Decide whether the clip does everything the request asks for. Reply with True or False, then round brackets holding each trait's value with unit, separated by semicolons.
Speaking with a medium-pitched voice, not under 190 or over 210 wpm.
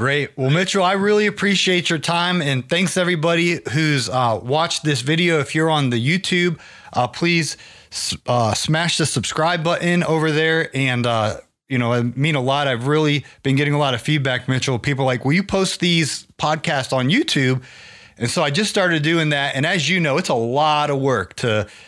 True (150 Hz; 205 wpm)